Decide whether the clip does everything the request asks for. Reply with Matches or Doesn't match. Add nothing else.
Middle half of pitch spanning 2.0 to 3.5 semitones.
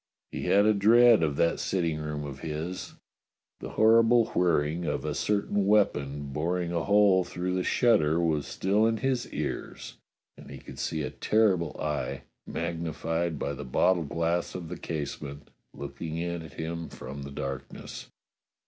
Doesn't match